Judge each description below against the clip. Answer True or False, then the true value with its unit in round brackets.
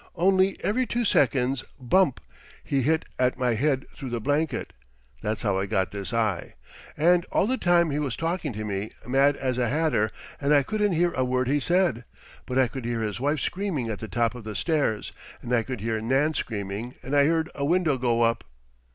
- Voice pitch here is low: True (130 Hz)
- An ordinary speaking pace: False (210 wpm)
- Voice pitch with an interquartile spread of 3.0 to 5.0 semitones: False (5.6 semitones)